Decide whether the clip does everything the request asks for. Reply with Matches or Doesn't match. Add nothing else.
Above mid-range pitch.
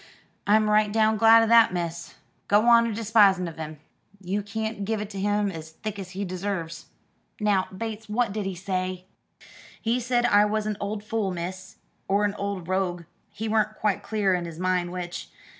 Matches